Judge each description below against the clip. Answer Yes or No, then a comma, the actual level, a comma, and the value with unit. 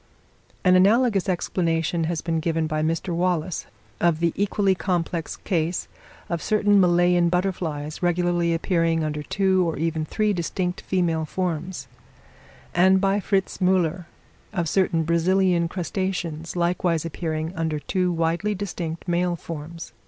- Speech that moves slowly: Yes, slow, 130 wpm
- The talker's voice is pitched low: No, medium, 175 Hz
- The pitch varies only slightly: Yes, narrow, 2.2 semitones